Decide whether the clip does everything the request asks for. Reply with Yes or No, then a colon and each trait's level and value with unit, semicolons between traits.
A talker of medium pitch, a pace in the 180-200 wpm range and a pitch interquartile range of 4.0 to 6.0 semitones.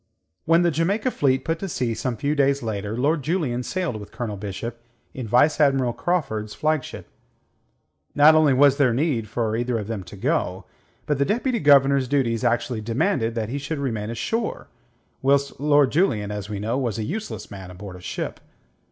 No: low, 130 Hz; average, 185 wpm; average, 5.1 semitones